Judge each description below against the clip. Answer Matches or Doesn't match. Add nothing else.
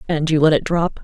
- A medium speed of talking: Doesn't match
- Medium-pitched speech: Matches